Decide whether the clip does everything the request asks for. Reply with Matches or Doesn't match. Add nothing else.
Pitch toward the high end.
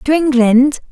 Matches